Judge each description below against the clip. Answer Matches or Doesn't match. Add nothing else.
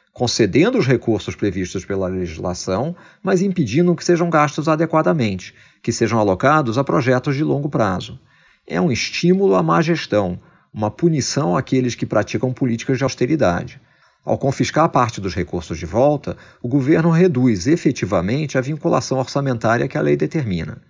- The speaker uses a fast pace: Doesn't match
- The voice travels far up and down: Matches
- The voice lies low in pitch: Matches